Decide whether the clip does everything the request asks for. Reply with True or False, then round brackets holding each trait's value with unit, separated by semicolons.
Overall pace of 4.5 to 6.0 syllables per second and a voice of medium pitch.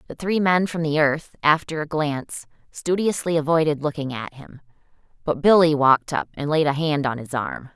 True (5.2 syllables/s; 150 Hz)